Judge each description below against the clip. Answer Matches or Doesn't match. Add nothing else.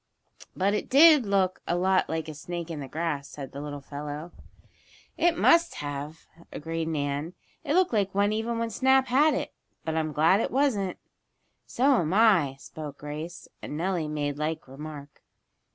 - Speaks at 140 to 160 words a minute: Doesn't match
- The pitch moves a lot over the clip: Matches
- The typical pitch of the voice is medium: Matches